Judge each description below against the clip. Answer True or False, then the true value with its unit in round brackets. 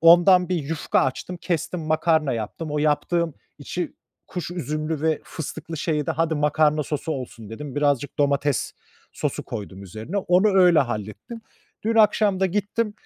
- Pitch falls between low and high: True (155 Hz)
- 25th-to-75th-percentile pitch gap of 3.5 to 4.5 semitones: True (3.8 semitones)